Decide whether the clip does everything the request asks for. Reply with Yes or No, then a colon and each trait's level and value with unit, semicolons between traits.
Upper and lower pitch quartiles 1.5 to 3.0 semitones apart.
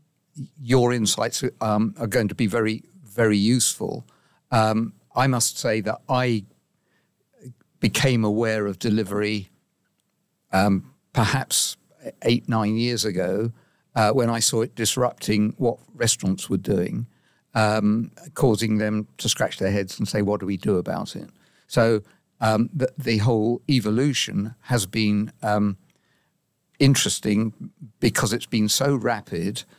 Yes: average, 2.7 semitones